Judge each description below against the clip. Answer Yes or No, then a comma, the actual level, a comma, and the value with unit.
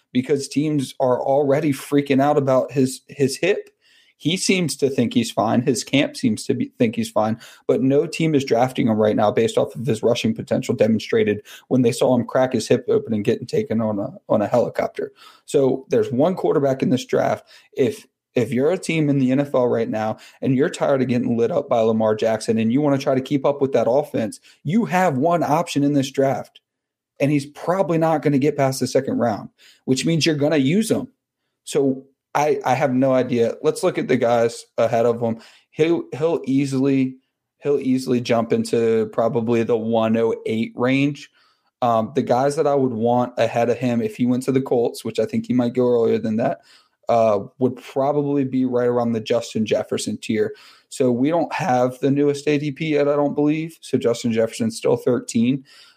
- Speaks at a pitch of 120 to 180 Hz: Yes, low, 135 Hz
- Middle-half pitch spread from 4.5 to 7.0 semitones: No, average, 3.6 semitones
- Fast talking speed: Yes, fast, 210 wpm